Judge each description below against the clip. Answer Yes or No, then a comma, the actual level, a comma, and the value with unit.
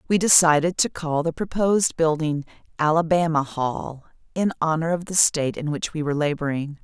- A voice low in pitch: No, medium, 160 Hz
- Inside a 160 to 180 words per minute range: Yes, average, 165 wpm